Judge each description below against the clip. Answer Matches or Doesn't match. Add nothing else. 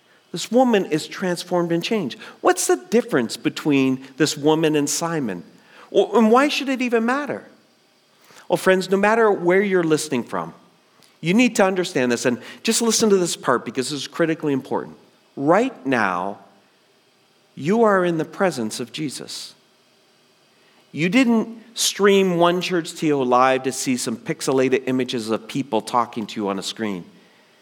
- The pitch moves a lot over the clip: Matches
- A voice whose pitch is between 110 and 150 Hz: Doesn't match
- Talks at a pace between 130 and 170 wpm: Matches